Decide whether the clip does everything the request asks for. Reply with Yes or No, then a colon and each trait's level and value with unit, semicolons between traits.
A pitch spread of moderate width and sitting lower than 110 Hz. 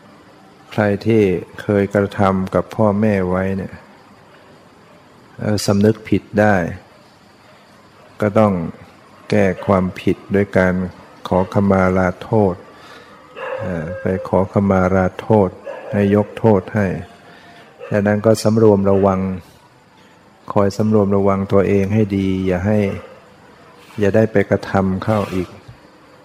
No: narrow, 1.9 semitones; low, 100 Hz